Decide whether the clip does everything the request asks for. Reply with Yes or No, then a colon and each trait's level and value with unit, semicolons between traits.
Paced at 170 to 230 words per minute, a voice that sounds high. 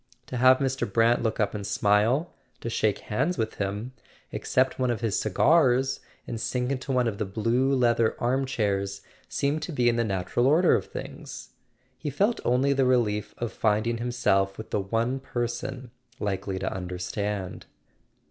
No: average, 175 wpm; low, 120 Hz